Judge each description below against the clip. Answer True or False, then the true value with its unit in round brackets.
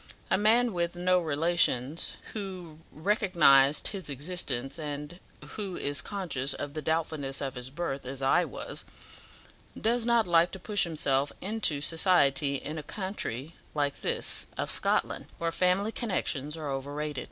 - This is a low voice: False (160 Hz)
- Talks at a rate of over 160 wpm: False (145 wpm)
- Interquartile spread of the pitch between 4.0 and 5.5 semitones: True (4.5 semitones)